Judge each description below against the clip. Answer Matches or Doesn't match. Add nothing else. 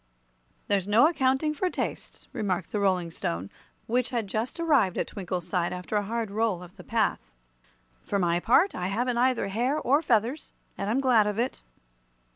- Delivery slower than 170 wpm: Doesn't match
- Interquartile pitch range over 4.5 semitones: Matches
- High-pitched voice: Matches